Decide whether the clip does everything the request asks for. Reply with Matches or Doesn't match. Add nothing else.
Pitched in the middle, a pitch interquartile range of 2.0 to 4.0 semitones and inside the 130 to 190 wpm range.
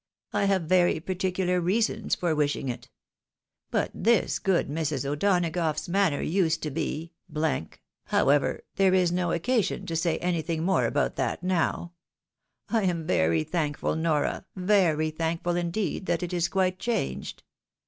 Matches